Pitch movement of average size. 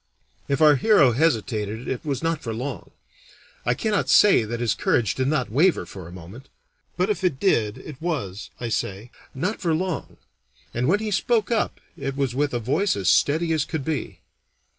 No: wide, 6.1 semitones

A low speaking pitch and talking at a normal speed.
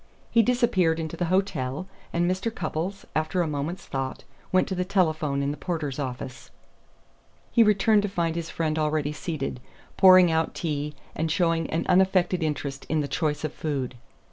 No: medium, 160 Hz; average, 170 wpm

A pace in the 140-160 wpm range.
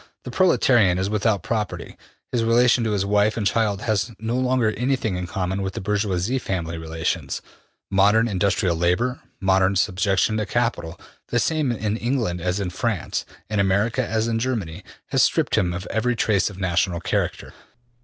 No: average, 170 wpm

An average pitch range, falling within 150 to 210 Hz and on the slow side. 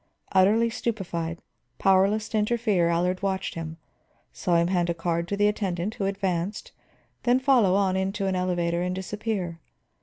No: average, 3.2 semitones; high, 190 Hz; average, 155 wpm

